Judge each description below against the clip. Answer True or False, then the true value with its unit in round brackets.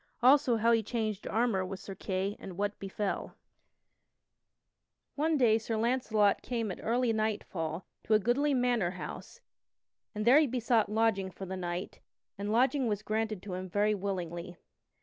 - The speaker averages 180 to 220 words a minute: False (160 wpm)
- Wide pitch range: False (3.7 semitones)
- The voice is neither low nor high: False (215 Hz)